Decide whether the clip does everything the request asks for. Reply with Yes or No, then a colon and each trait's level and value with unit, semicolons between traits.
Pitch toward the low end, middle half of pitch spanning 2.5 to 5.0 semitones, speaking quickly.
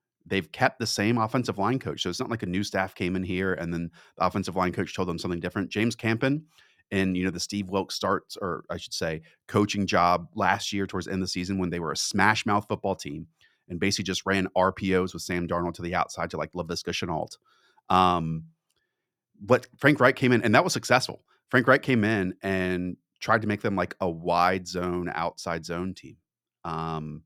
Yes: very low, 95 Hz; average, 2.8 semitones; fast, 220 wpm